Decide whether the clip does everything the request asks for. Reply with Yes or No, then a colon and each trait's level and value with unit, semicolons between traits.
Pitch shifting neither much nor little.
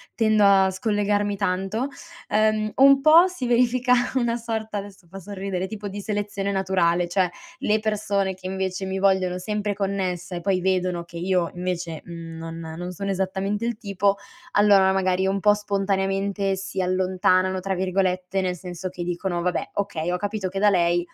No: narrow, 2.0 semitones